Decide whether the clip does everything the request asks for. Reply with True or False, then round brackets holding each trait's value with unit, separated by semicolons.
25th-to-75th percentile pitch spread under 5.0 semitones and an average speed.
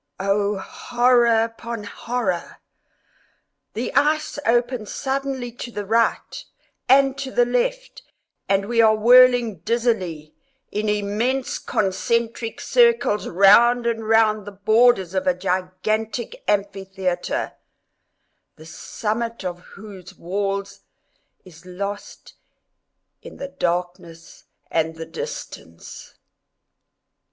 False (4.0 semitones; 100 wpm)